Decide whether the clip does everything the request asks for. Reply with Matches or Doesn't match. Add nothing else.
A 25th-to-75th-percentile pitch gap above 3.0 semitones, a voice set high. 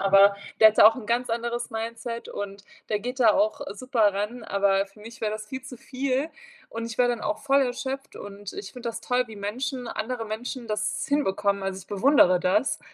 Matches